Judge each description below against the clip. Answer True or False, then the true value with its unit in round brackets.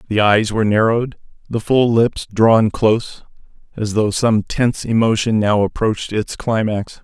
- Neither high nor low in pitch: False (110 Hz)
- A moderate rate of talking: True (155 wpm)